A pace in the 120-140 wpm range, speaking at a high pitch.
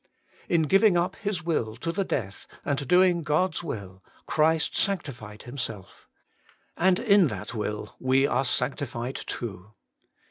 No: slow, 135 wpm; medium, 140 Hz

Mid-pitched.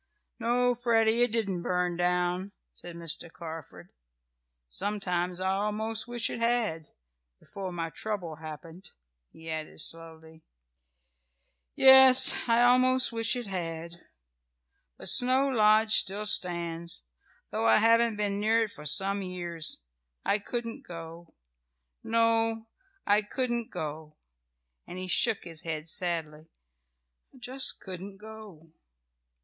No: high, 195 Hz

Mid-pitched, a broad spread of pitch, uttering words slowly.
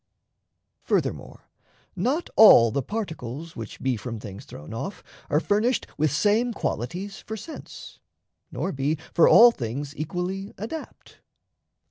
Yes: medium, 165 Hz; wide, 8.6 semitones; slow, 125 wpm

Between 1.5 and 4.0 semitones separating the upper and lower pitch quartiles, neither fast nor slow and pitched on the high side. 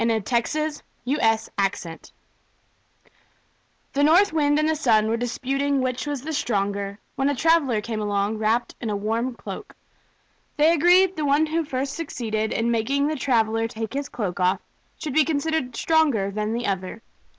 No: average, 5.2 semitones; average, 160 wpm; high, 245 Hz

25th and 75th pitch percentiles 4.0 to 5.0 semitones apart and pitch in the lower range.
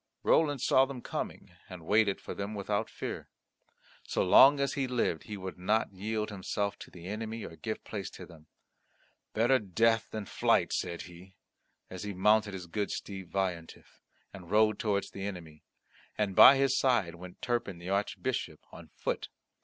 No: average, 3.2 semitones; low, 100 Hz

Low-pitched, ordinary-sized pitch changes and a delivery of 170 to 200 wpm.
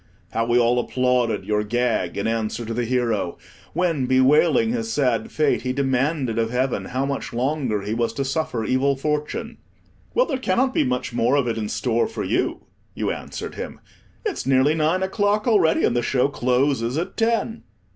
Yes: low, 130 Hz; average, 4.6 semitones; average, 185 wpm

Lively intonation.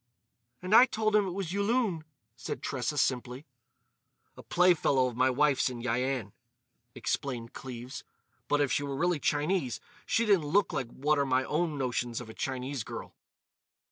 Yes: wide, 5.7 semitones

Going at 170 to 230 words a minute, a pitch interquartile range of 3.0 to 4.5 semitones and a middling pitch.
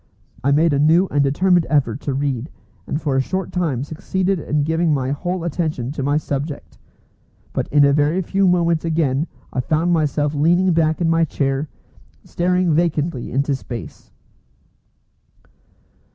No: average, 155 wpm; average, 3.3 semitones; medium, 155 Hz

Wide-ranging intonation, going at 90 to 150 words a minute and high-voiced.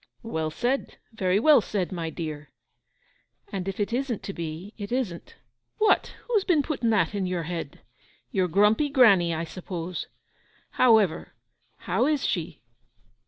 Yes: wide, 6.0 semitones; average, 140 wpm; high, 195 Hz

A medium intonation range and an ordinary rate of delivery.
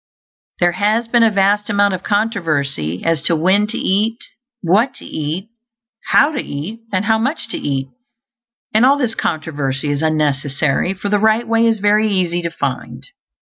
No: wide, 6.0 semitones; average, 175 wpm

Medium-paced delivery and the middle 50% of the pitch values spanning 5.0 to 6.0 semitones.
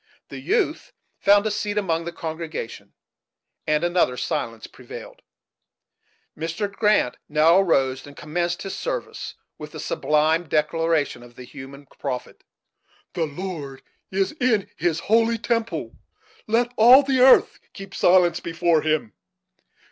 No: slow, 130 wpm; wide, 5.5 semitones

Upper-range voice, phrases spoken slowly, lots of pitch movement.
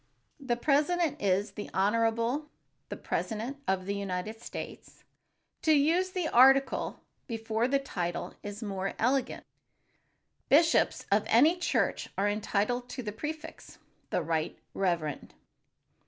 Yes: high, 230 Hz; slow, 125 wpm; wide, 5.8 semitones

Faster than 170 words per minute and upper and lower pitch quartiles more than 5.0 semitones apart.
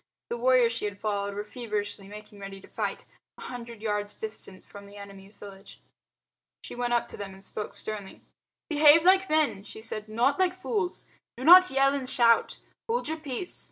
Yes: average, 190 wpm; wide, 5.4 semitones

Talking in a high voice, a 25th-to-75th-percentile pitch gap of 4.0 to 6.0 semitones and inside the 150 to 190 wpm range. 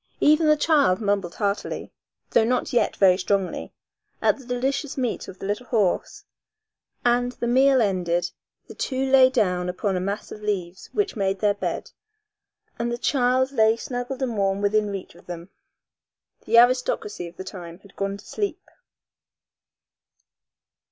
Yes: high, 215 Hz; average, 4.6 semitones; average, 160 wpm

